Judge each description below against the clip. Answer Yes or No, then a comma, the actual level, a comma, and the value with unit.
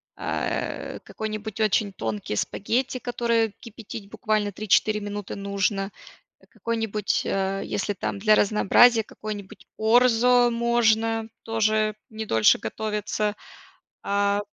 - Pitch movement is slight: Yes, narrow, 1.9 semitones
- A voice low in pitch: No, high, 215 Hz